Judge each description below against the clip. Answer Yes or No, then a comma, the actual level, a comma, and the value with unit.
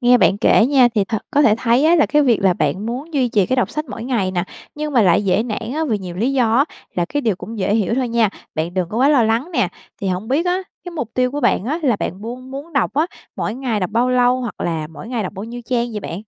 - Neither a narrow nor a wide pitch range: Yes, average, 4.5 semitones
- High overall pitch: Yes, high, 235 Hz